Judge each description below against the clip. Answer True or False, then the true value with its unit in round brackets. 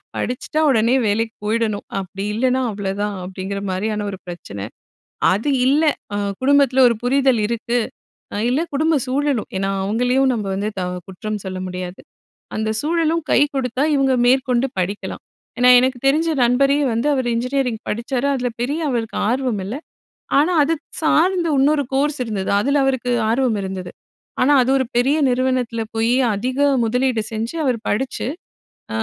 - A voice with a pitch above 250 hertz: False (245 Hz)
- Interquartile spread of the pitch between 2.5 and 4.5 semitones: True (4.1 semitones)